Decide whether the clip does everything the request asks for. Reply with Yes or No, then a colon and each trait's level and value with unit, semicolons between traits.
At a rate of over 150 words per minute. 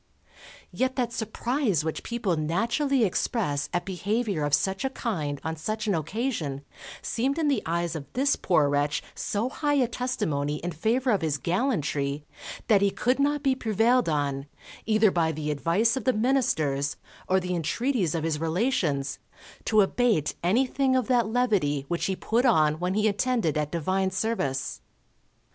Yes: average, 165 wpm